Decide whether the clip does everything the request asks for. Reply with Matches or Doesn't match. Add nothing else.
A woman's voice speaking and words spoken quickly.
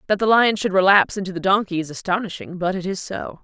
Matches